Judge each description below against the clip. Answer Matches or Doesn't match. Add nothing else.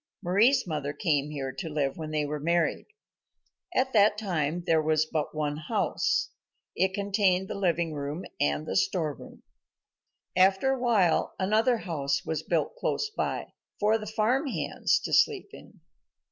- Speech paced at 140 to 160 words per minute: Matches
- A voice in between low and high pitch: Matches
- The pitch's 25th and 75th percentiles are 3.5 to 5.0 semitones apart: Doesn't match